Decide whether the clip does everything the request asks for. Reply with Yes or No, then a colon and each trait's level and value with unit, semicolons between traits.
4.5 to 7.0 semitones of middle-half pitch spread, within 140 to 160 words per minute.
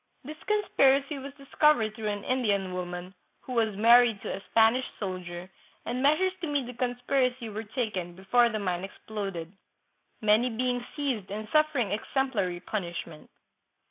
Yes: average, 5.0 semitones; average, 150 wpm